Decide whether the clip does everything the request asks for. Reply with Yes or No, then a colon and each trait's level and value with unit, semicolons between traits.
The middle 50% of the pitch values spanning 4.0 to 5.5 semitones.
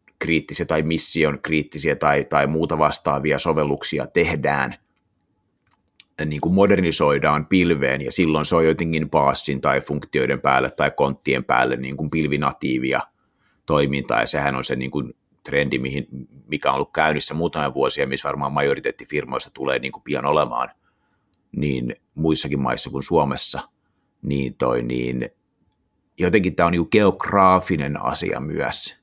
No: average, 2.8 semitones